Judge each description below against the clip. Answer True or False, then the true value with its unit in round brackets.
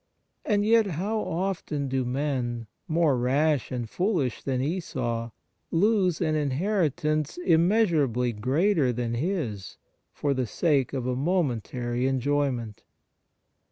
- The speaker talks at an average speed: False (120 wpm)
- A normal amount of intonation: False (5.7 semitones)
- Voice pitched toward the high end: False (145 Hz)